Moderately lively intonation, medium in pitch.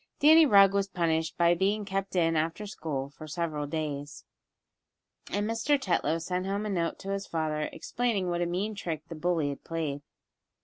Yes: average, 3.9 semitones; medium, 175 Hz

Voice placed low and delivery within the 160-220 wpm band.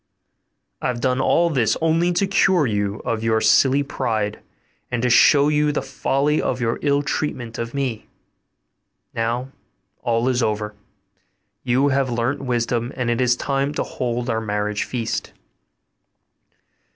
No: low, 125 Hz; average, 150 wpm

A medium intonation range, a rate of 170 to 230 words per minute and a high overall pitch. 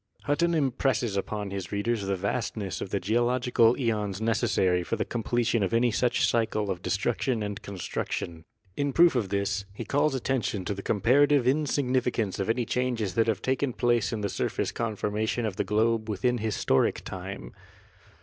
No: average, 3.5 semitones; average, 175 wpm; low, 115 Hz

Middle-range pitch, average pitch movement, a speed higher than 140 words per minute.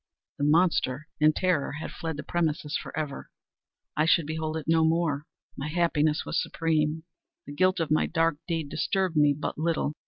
No: medium, 155 Hz; narrow, 1.7 semitones; average, 175 wpm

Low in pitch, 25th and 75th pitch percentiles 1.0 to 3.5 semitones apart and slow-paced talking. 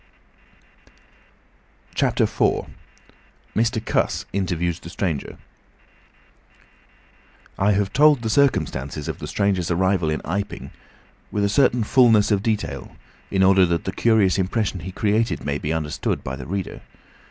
No: very low, 95 Hz; average, 4.2 semitones; slow, 130 wpm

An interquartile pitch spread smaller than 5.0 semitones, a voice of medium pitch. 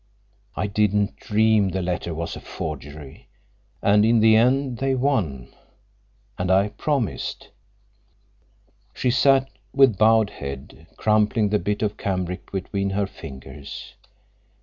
No: average, 3.7 semitones; low, 105 Hz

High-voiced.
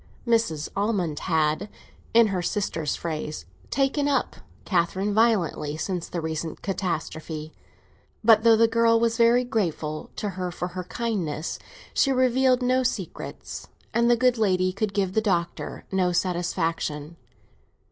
Yes: high, 195 Hz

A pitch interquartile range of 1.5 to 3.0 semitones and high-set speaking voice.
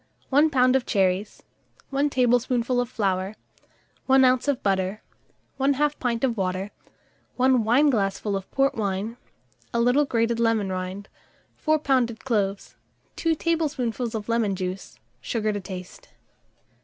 No: average, 4.9 semitones; high, 235 Hz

